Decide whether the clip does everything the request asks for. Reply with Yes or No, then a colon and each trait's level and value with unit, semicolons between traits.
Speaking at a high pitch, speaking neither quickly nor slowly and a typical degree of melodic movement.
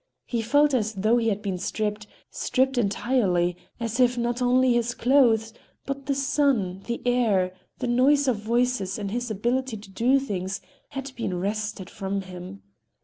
Yes: high, 230 Hz; average, 160 wpm; average, 4.1 semitones